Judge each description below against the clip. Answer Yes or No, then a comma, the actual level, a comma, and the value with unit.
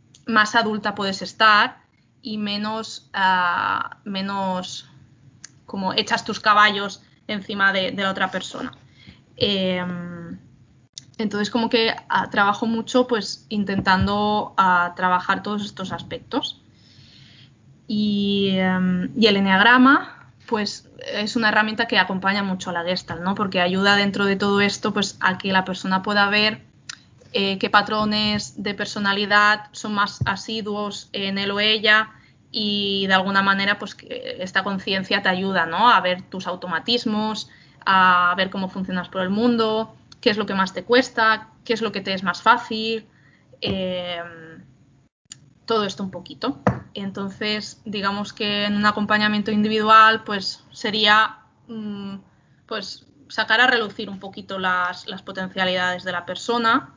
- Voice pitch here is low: No, high, 205 Hz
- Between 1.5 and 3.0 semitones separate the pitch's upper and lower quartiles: Yes, narrow, 2.4 semitones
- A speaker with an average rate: Yes, average, 140 wpm